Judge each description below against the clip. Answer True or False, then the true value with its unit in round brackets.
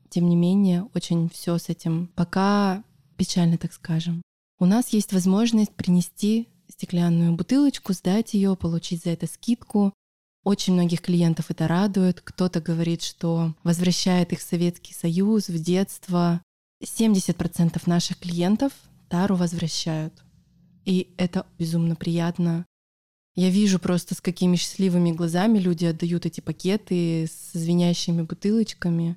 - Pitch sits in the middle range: True (175 Hz)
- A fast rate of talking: False (130 wpm)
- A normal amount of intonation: False (2.0 semitones)